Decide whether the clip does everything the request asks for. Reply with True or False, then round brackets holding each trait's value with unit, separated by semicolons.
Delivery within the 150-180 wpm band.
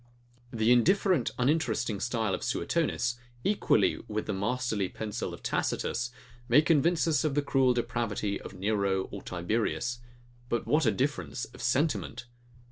False (140 wpm)